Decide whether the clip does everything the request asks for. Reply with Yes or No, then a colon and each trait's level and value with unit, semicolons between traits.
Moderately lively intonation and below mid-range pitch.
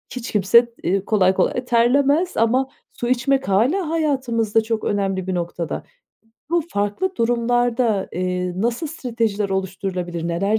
No: average, 4.7 semitones; high, 230 Hz